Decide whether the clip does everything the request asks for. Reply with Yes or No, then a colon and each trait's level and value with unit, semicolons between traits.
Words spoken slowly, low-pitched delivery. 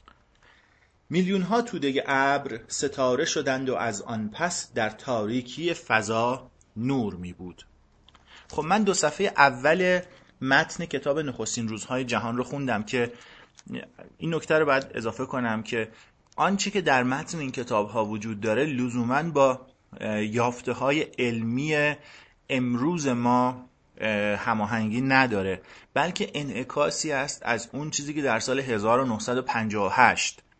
No: average, 125 wpm; low, 125 Hz